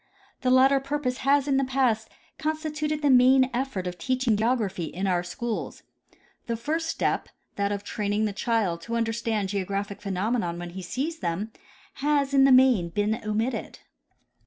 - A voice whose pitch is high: Yes, high, 230 Hz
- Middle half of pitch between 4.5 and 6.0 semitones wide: Yes, average, 5.0 semitones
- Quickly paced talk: No, average, 165 wpm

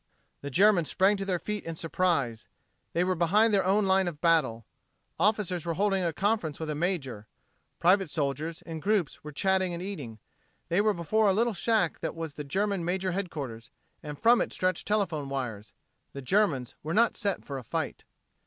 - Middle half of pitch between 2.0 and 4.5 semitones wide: No, average, 5.0 semitones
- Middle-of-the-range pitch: Yes, medium, 175 Hz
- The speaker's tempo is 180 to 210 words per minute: Yes, average, 190 wpm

